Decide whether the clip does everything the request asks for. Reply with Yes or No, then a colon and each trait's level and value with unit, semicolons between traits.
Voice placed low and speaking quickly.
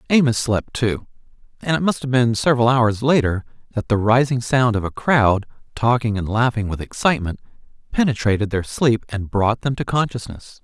No: low, 120 Hz; average, 175 wpm